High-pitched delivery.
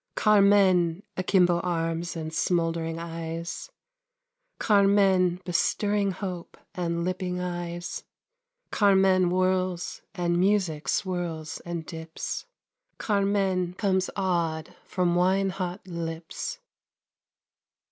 No: medium, 180 Hz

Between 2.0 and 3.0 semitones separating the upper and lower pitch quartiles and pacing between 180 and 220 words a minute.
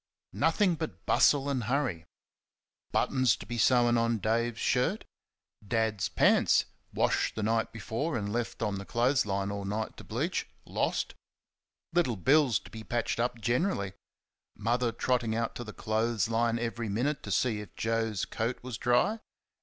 No: narrow, 2.5 semitones; average, 160 wpm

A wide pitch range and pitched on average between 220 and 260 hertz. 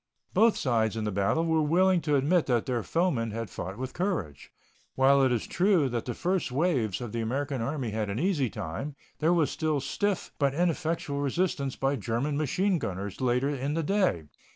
No: wide, 6.2 semitones; medium, 140 Hz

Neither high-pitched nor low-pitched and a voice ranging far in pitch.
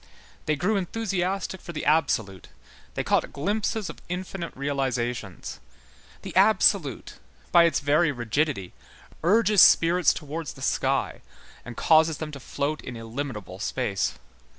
Yes: medium, 150 Hz; wide, 5.9 semitones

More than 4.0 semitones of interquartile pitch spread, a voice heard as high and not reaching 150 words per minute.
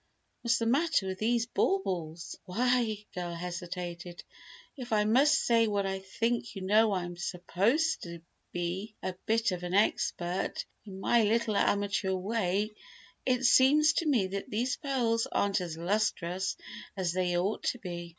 No: average, 4.5 semitones; high, 200 Hz; average, 160 wpm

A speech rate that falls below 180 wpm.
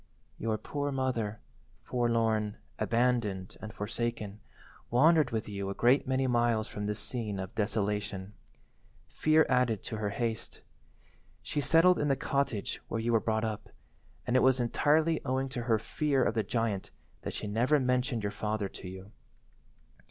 Yes: average, 160 wpm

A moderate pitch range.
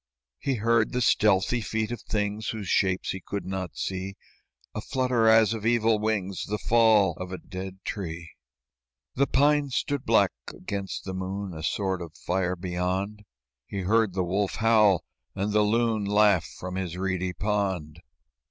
Yes: average, 3.0 semitones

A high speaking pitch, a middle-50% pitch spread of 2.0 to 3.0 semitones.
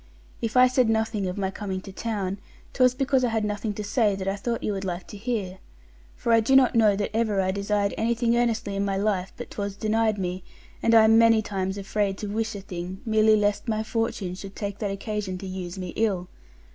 Yes: high, 210 Hz; narrow, 2.6 semitones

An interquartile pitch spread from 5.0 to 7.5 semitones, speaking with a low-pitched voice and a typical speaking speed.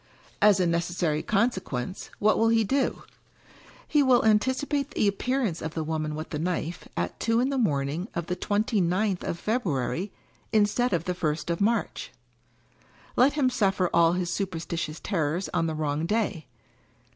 No: average, 5.3 semitones; medium, 185 Hz; average, 170 wpm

